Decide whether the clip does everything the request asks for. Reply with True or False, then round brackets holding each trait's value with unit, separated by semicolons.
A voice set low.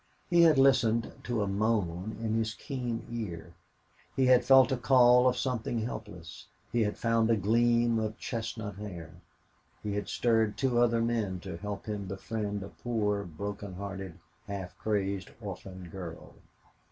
True (110 Hz)